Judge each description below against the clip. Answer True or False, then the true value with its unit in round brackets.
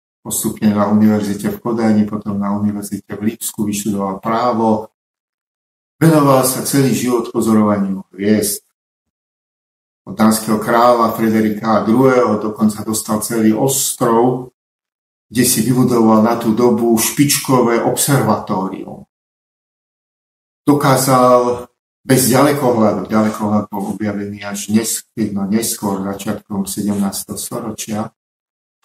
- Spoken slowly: True (95 wpm)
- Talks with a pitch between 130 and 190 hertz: False (110 Hz)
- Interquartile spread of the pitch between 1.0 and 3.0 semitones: True (2.7 semitones)